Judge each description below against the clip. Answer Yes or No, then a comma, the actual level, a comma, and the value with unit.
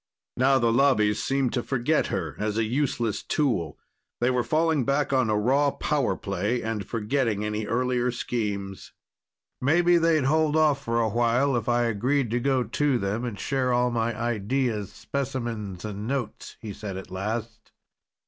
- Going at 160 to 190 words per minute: Yes, average, 165 wpm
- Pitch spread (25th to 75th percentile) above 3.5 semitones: Yes, average, 4.1 semitones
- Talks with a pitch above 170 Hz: No, low, 120 Hz